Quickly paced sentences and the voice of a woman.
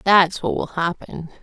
No: average, 170 wpm; female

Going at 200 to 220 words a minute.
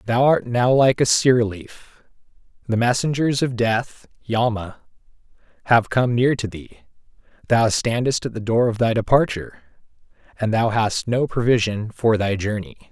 No: average, 155 wpm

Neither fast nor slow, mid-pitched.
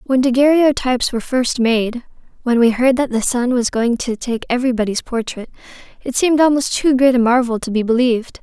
No: average, 190 wpm; high, 245 Hz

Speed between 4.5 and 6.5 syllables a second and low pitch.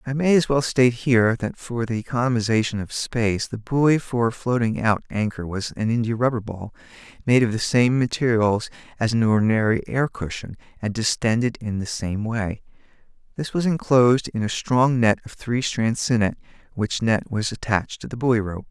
Yes: 5.1 syllables/s; low, 115 Hz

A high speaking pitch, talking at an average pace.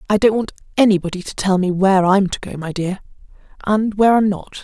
No: high, 195 Hz; fast, 220 wpm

